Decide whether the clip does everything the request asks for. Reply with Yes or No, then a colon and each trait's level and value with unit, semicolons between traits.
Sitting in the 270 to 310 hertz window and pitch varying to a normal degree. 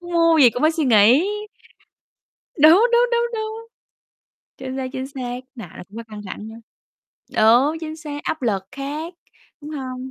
Yes: very high, 280 Hz; average, 4.8 semitones